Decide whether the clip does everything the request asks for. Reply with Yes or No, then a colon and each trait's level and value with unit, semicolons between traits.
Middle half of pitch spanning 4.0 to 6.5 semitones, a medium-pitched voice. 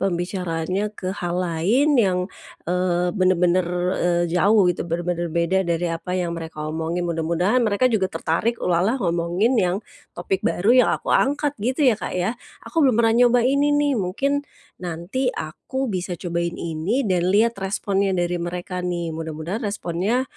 Yes: average, 4.5 semitones; medium, 180 Hz